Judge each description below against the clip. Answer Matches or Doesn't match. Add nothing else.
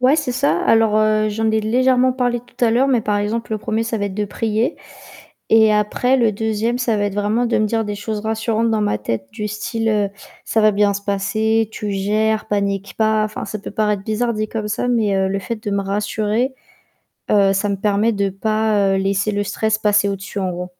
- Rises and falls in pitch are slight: Matches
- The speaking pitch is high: Matches